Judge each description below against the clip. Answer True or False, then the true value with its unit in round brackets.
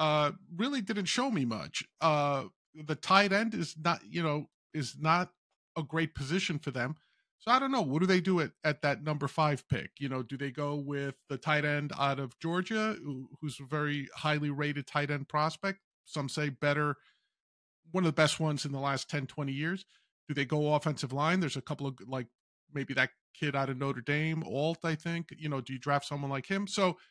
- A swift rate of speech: True (220 wpm)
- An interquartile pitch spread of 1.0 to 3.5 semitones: True (2.9 semitones)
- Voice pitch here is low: False (150 Hz)